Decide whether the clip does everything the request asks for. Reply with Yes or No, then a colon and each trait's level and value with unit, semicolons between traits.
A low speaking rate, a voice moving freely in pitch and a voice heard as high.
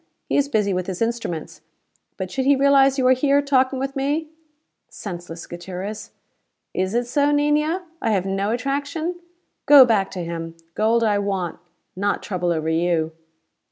No: average, 165 wpm; wide, 7.3 semitones; high, 225 Hz